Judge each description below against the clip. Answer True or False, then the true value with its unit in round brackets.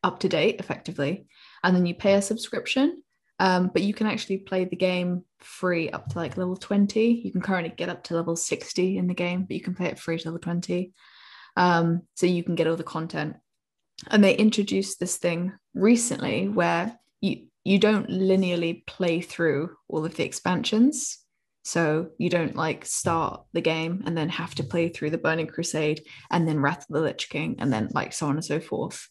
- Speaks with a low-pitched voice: False (180 Hz)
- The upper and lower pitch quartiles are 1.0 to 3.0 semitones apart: True (2.7 semitones)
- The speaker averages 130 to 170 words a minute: False (205 wpm)